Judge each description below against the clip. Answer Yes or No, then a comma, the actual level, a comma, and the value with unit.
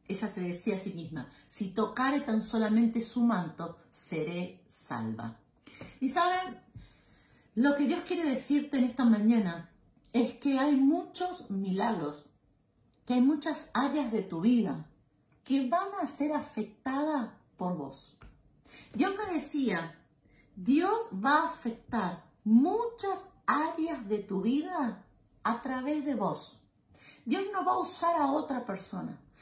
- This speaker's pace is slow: No, average, 135 wpm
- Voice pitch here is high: Yes, high, 245 Hz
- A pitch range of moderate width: No, wide, 7.4 semitones